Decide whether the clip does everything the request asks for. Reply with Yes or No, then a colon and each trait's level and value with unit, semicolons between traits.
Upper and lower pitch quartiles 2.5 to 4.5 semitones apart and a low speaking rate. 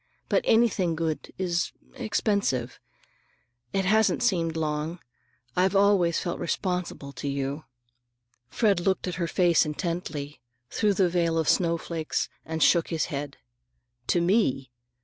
Yes: average, 3.5 semitones; slow, 125 wpm